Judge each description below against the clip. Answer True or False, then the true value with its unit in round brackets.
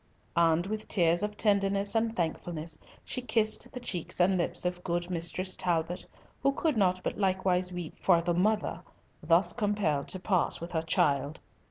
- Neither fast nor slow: True (170 wpm)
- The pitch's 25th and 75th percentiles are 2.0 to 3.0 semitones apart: False (3.5 semitones)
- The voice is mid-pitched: True (180 Hz)